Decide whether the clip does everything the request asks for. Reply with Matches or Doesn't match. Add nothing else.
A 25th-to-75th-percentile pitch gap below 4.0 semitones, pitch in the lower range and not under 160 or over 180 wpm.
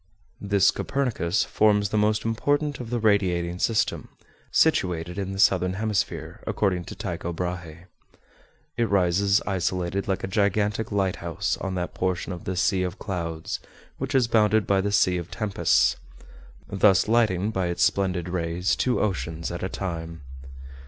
Doesn't match